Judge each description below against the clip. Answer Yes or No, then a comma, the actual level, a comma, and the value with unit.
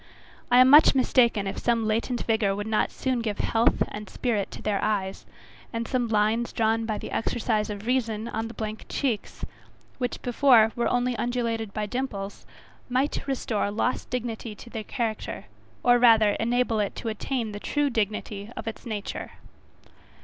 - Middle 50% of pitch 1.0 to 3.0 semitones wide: Yes, narrow, 2.4 semitones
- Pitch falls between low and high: No, high, 225 Hz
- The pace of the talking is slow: No, average, 170 wpm